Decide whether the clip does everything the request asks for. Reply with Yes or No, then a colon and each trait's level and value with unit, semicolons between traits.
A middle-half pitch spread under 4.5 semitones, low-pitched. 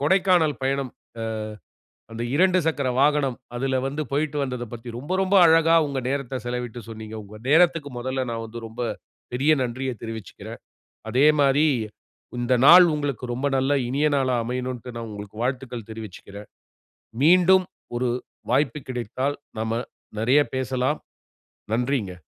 Yes: average, 3.5 semitones; low, 130 Hz